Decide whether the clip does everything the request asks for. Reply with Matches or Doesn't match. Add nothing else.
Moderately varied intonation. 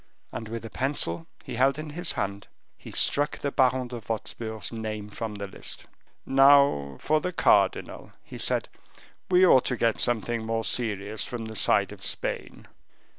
Matches